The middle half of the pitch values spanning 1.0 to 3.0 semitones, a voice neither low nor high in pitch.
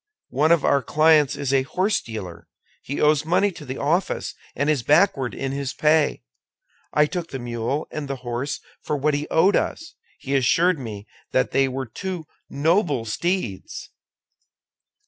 No: average, 3.9 semitones; medium, 145 Hz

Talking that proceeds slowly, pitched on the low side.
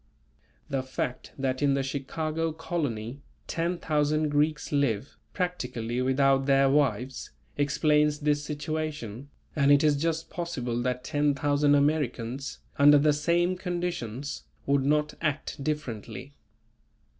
No: slow, 115 wpm; medium, 145 Hz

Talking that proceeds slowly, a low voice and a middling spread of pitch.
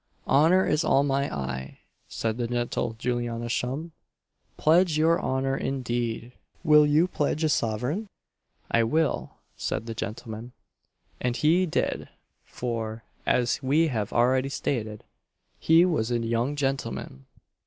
Yes: slow, 130 wpm; low, 125 Hz; average, 4.6 semitones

